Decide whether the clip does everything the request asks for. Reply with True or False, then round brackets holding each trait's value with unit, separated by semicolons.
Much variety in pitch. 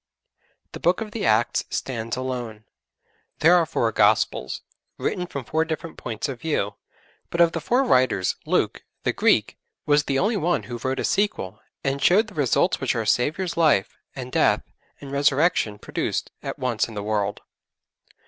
True (6.4 semitones)